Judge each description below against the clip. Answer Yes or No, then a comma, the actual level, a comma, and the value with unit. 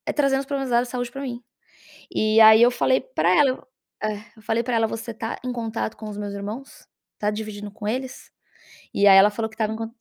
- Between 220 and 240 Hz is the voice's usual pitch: Yes, high, 225 Hz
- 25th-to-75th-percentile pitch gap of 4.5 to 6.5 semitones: No, average, 2.8 semitones